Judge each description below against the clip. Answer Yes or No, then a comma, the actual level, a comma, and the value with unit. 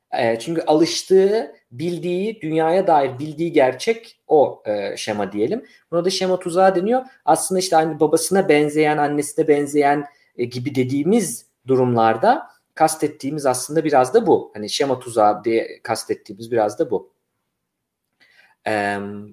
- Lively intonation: Yes, wide, 6.3 semitones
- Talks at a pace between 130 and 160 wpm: No, average, 120 wpm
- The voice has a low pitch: No, medium, 150 Hz